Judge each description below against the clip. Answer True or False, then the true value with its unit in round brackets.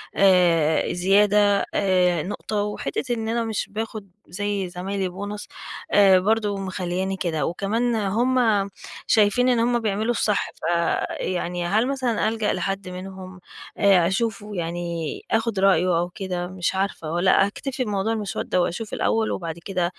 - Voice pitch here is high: True (195 Hz)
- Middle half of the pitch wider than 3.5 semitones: False (3.2 semitones)